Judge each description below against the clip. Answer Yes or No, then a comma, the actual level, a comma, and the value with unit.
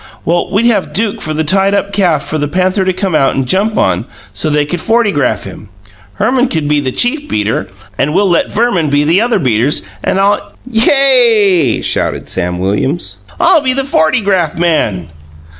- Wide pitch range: Yes, wide, 6.6 semitones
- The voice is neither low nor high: Yes, medium, 180 Hz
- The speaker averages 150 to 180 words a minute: No, average, 190 wpm